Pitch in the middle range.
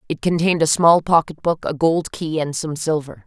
Yes: medium, 160 Hz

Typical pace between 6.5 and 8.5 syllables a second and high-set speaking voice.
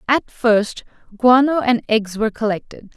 No: 4.5 syllables/s; high, 230 Hz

